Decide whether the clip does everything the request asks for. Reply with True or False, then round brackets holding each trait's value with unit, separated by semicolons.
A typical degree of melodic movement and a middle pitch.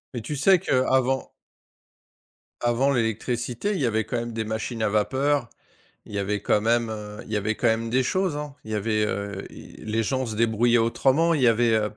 False (3.2 semitones; 115 Hz)